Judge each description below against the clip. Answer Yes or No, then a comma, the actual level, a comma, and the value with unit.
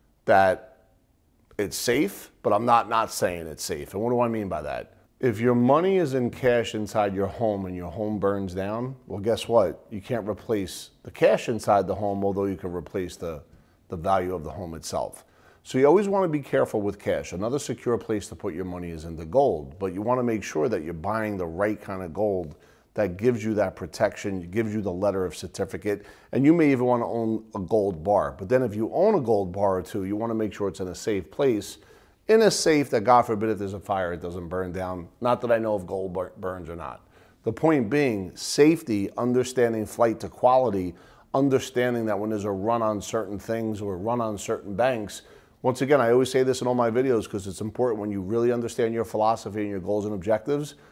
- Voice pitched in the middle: No, low, 110 Hz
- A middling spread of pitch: Yes, average, 3.9 semitones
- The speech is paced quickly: Yes, fast, 235 wpm